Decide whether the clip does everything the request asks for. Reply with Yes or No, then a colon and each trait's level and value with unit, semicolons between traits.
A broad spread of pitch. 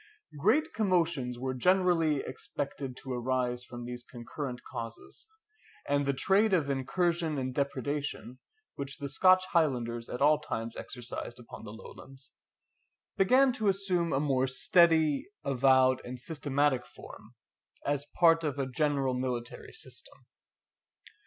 No: average, 4.4 semitones